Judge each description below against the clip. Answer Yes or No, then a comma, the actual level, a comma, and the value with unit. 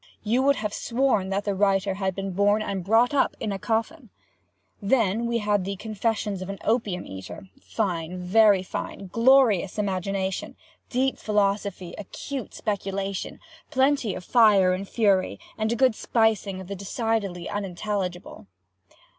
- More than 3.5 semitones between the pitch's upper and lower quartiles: No, average, 2.9 semitones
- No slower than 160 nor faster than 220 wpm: No, slow, 135 wpm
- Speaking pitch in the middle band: No, high, 200 Hz